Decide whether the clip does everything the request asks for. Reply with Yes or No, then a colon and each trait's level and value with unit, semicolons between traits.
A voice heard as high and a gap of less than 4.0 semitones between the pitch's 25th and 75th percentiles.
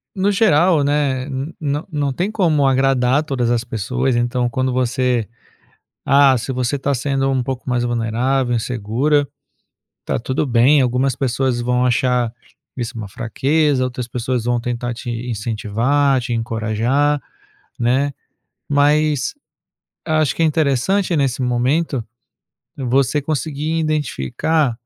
No: low, 130 Hz; average, 3.1 semitones